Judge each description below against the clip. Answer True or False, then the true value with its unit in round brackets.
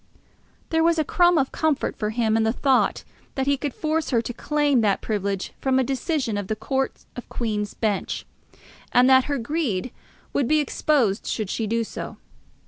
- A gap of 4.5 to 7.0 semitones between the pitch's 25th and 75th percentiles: True (5.0 semitones)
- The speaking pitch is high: True (255 Hz)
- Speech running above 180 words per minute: True (190 wpm)